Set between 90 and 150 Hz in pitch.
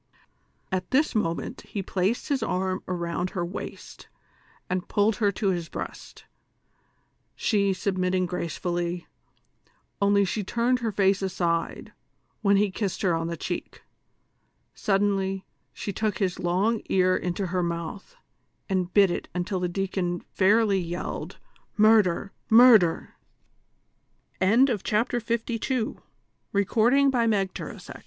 No: high, 190 Hz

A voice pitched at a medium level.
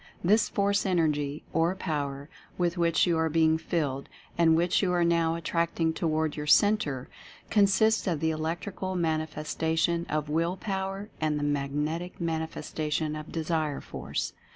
Yes: medium, 165 Hz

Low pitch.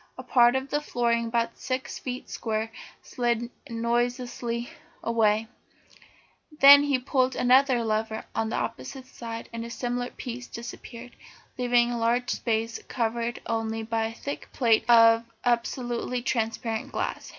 No: high, 235 Hz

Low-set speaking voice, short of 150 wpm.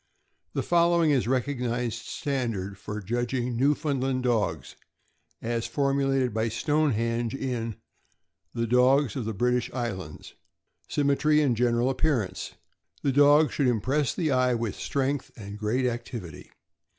Yes: low, 125 Hz; average, 140 wpm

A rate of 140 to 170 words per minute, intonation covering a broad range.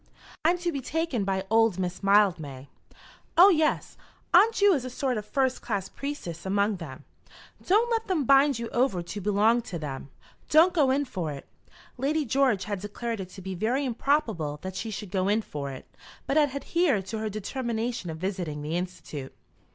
No: average, 190 wpm; wide, 7.0 semitones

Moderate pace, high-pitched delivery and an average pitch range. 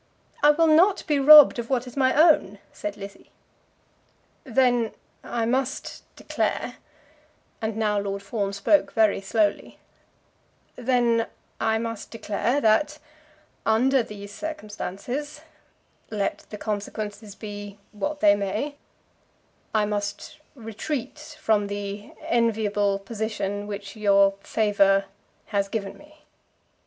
No: slow, 115 wpm; high, 220 Hz; average, 3.7 semitones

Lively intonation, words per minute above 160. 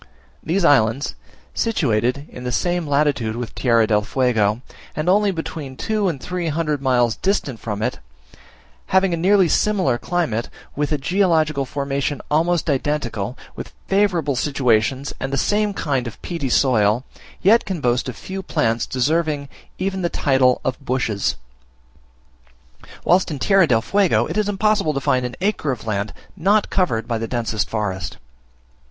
No: wide, 6.6 semitones; average, 155 wpm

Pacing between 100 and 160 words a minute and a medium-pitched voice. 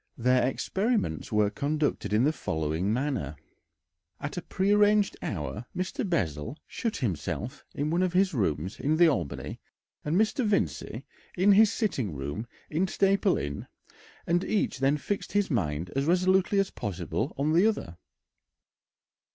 Yes: average, 145 wpm; medium, 145 Hz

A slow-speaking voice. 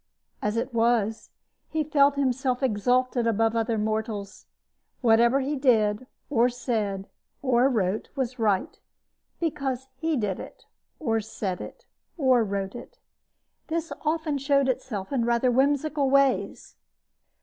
Yes: slow, 125 wpm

